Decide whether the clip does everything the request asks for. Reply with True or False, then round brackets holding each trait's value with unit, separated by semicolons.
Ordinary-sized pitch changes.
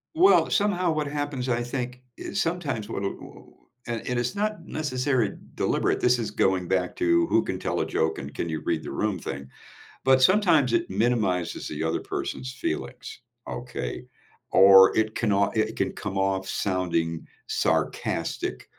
False (7.0 semitones)